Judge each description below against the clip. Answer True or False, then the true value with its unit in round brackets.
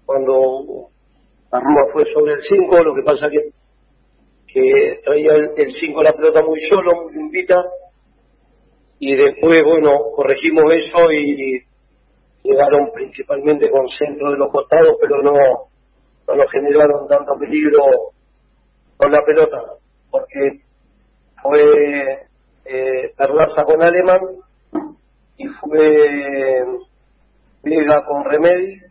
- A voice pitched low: False (160 Hz)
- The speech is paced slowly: True (115 wpm)